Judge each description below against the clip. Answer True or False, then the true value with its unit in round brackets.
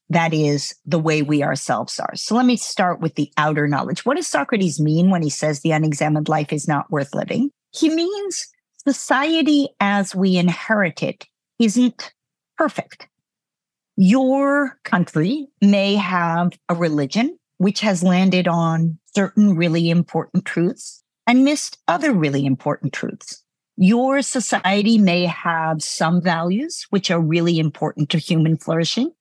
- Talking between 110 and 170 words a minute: True (145 wpm)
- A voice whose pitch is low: False (180 Hz)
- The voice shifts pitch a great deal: True (6.1 semitones)